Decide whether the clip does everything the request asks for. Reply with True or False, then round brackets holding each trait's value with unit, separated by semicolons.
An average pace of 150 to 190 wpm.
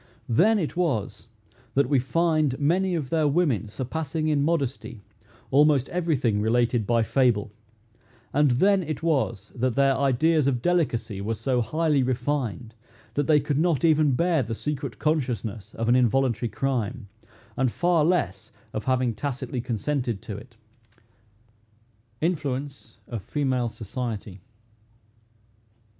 False (135 wpm)